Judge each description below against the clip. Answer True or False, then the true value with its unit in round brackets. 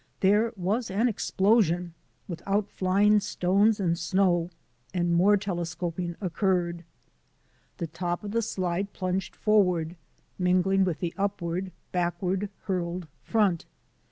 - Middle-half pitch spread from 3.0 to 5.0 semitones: False (2.5 semitones)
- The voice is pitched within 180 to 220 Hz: True (185 Hz)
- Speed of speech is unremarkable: False (120 wpm)